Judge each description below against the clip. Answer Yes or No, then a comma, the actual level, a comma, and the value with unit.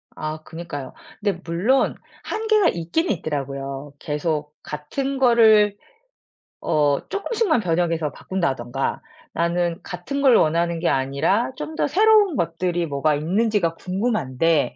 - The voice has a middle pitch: Yes, medium, 170 Hz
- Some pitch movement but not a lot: No, wide, 7.3 semitones